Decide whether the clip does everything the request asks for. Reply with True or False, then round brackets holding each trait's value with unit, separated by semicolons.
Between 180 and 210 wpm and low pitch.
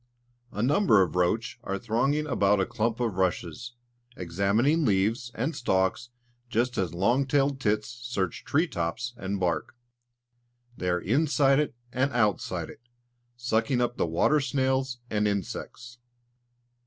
False (140 wpm; 120 Hz)